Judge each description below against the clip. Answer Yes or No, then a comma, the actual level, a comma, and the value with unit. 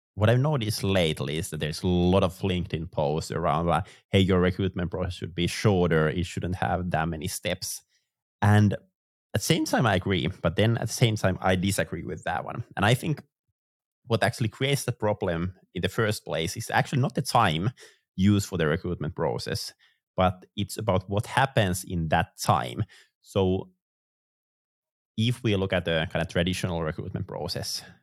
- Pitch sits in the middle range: No, very low, 95 Hz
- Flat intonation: No, average, 3.9 semitones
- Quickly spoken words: No, average, 185 wpm